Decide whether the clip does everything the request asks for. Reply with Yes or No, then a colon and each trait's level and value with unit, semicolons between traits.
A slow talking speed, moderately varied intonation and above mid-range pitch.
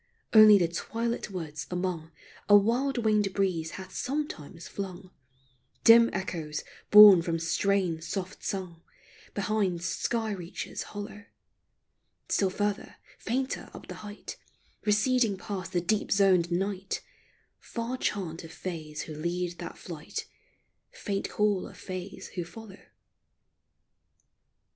Yes: slow, 120 wpm; average, 3.4 semitones; high, 195 Hz